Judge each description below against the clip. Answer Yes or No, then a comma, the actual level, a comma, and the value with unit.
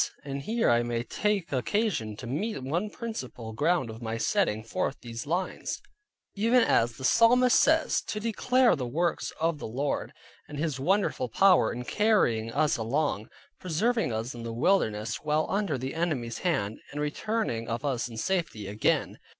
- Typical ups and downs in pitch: No, wide, 9.0 semitones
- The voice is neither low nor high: Yes, medium, 145 Hz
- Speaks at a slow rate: No, average, 165 wpm